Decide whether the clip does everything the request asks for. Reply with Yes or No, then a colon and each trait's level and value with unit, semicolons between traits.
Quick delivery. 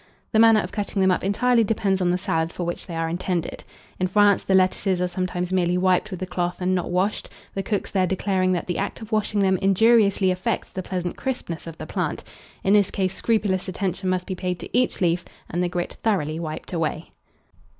Yes: fast, 220 wpm